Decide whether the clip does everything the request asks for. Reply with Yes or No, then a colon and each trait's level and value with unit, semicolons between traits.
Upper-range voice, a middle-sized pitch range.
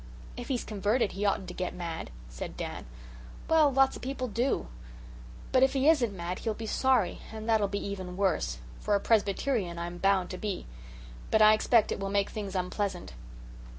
Yes: high, 205 Hz; average, 4.3 semitones